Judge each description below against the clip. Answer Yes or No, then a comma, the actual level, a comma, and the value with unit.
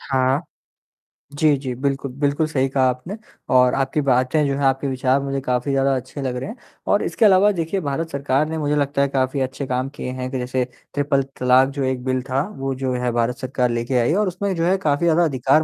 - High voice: No, low, 135 Hz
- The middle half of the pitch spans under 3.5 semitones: Yes, narrow, 2.4 semitones